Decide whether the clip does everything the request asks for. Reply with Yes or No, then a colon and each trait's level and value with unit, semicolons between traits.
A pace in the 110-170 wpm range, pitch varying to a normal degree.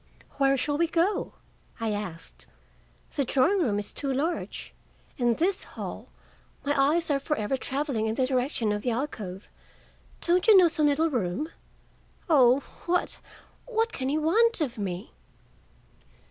No: average, 150 wpm; wide, 5.9 semitones